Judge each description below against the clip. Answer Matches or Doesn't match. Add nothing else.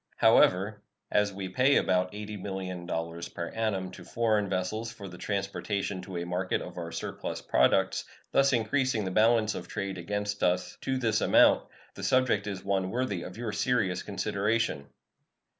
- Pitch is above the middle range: Doesn't match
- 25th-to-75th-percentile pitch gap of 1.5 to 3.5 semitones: Matches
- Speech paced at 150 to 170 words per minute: Matches